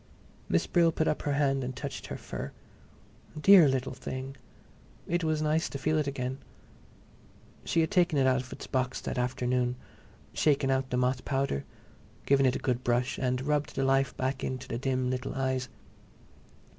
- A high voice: No, low, 135 Hz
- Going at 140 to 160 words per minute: No, average, 180 wpm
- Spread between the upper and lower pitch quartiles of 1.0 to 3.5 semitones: Yes, narrow, 2.4 semitones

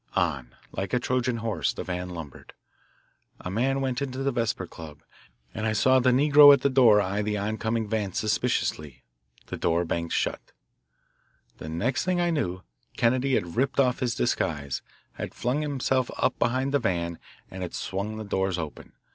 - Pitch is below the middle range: Yes, low, 110 Hz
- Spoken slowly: No, average, 175 wpm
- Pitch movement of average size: No, wide, 6.3 semitones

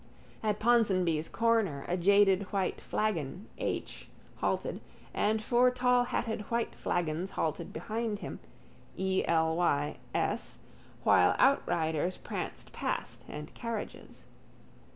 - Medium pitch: No, high, 200 Hz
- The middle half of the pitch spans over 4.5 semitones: Yes, average, 5.3 semitones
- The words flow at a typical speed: No, slow, 95 wpm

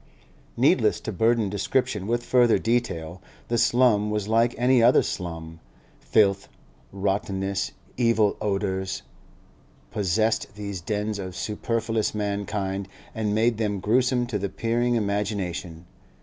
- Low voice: Yes, low, 105 Hz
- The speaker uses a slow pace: Yes, slow, 120 wpm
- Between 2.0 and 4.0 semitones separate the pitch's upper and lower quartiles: Yes, average, 2.9 semitones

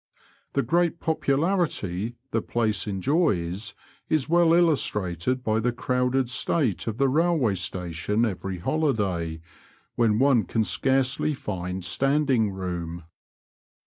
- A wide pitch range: Yes, wide, 6.7 semitones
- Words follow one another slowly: Yes, slow, 115 wpm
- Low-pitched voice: Yes, low, 115 Hz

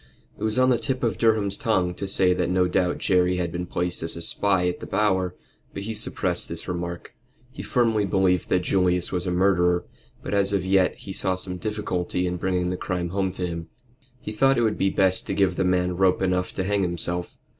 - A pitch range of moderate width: No, narrow, 1.9 semitones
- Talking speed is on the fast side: Yes, fast, 220 wpm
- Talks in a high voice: No, very low, 90 Hz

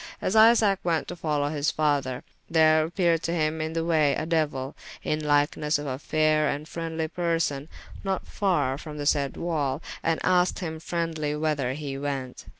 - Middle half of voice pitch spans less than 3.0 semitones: Yes, narrow, 2.4 semitones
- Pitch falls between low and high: Yes, medium, 155 Hz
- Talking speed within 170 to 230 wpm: Yes, average, 175 wpm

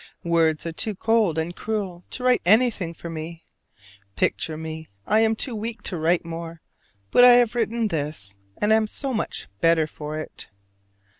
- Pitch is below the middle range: No, medium, 175 Hz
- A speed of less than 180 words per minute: Yes, average, 170 wpm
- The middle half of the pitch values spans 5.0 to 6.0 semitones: Yes, wide, 5.5 semitones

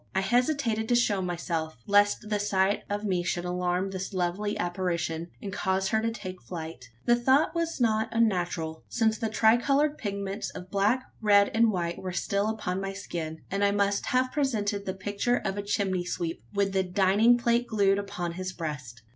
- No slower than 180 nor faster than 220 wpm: Yes, average, 185 wpm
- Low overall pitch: No, high, 200 Hz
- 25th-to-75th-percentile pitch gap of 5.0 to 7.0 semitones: No, average, 3.4 semitones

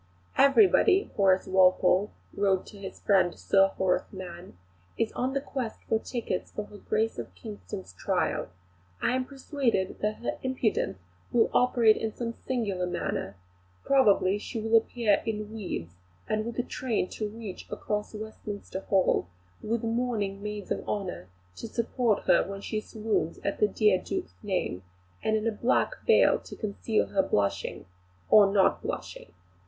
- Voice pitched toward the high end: Yes, high, 210 Hz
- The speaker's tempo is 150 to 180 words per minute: Yes, average, 155 wpm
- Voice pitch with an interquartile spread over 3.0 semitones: Yes, average, 3.4 semitones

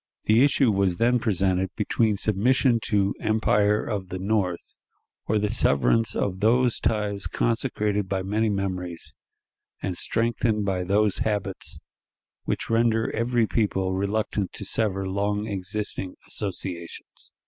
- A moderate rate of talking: No, slow, 125 wpm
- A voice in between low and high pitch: No, low, 105 Hz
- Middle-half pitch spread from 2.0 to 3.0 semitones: Yes, narrow, 2.6 semitones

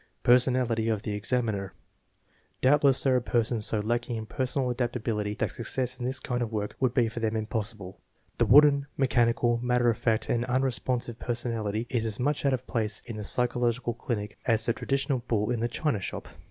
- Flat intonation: Yes, narrow, 2.3 semitones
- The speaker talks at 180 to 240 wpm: Yes, average, 190 wpm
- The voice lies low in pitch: Yes, low, 120 Hz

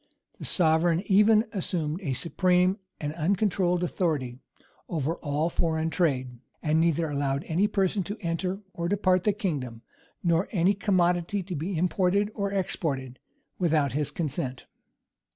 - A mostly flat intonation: No, average, 4.0 semitones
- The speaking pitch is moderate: Yes, medium, 170 Hz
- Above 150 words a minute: No, average, 140 wpm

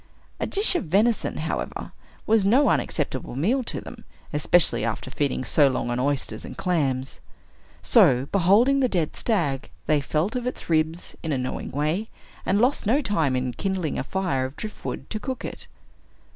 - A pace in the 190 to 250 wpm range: No, average, 170 wpm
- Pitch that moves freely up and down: Yes, wide, 7.8 semitones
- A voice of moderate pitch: Yes, medium, 170 Hz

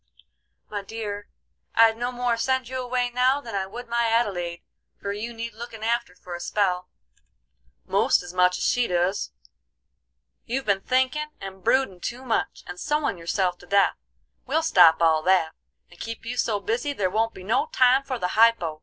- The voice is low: No, high, 225 Hz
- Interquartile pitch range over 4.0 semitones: Yes, average, 5.1 semitones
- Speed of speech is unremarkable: Yes, average, 180 wpm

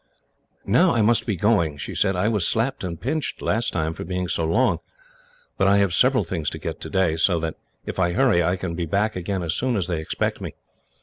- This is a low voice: Yes, very low, 95 Hz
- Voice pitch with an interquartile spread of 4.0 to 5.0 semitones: Yes, average, 4.6 semitones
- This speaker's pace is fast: Yes, fast, 230 wpm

